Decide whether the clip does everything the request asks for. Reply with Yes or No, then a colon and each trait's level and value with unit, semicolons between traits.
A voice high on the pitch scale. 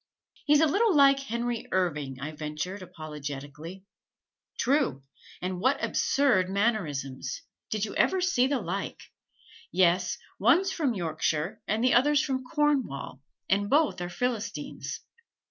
Yes: high, 205 Hz